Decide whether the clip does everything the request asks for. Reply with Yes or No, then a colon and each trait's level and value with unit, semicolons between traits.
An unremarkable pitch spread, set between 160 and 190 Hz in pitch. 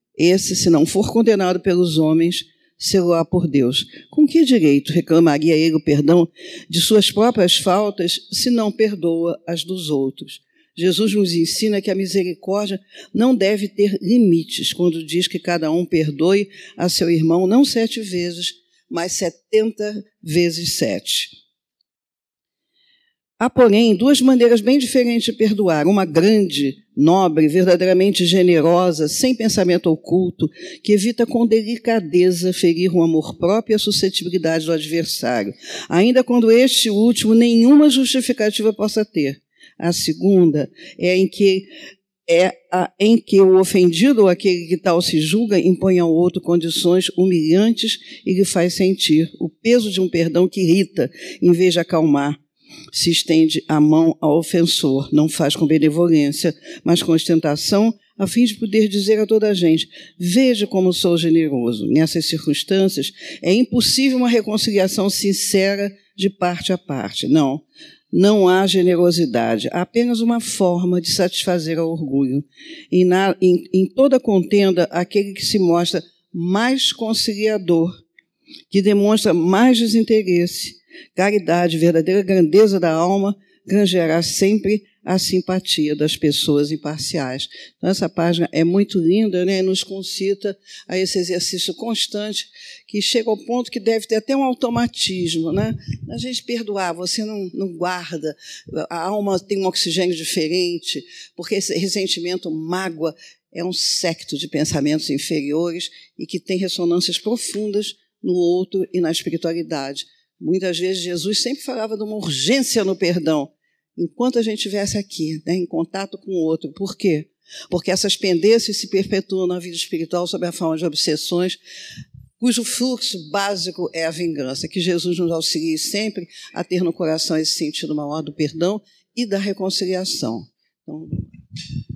Yes: average, 3.9 semitones; medium, 185 Hz